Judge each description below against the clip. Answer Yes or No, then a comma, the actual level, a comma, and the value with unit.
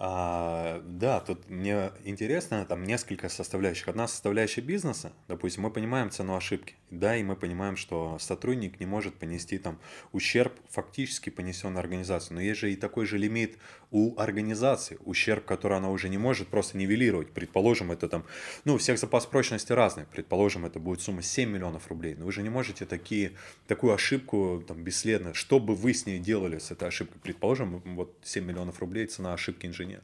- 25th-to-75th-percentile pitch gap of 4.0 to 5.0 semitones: No, average, 3.6 semitones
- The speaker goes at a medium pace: No, fast, 180 wpm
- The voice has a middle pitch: No, low, 100 Hz